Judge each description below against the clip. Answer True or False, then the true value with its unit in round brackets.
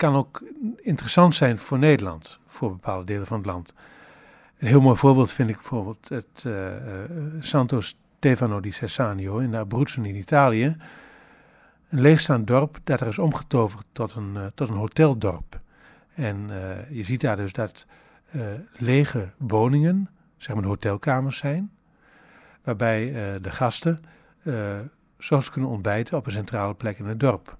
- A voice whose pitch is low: True (125 Hz)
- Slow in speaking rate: False (165 wpm)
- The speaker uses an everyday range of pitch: False (5.9 semitones)